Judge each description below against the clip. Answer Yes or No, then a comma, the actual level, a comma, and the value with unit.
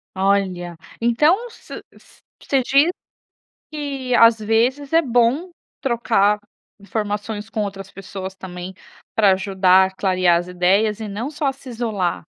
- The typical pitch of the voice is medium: No, high, 210 Hz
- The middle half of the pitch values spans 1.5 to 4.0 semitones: No, average, 4.9 semitones